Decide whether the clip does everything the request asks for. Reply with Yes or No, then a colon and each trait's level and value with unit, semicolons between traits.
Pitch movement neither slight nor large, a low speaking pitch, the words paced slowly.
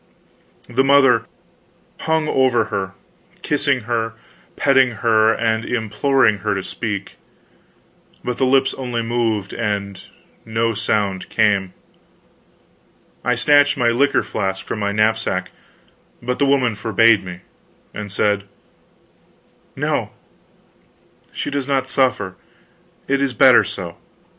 Yes: average, 4.2 semitones; low, 115 Hz; slow, 115 wpm